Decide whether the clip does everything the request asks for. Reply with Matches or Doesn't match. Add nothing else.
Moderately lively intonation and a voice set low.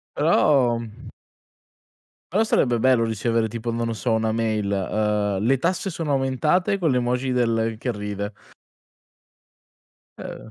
Matches